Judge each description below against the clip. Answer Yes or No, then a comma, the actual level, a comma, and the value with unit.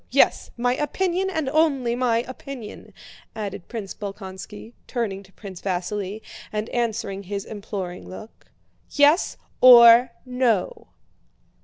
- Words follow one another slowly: Yes, slow, 115 wpm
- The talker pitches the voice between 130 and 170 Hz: No, high, 225 Hz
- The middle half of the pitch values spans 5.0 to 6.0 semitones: No, average, 4.2 semitones